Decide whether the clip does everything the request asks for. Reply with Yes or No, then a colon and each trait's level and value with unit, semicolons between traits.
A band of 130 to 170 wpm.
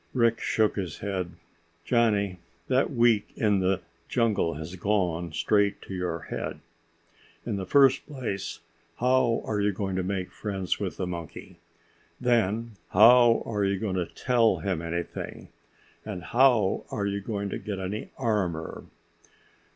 Yes: average, 145 wpm